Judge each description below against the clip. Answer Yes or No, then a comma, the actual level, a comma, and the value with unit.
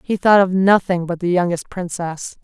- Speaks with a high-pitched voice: No, medium, 180 Hz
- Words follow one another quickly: No, average, 195 wpm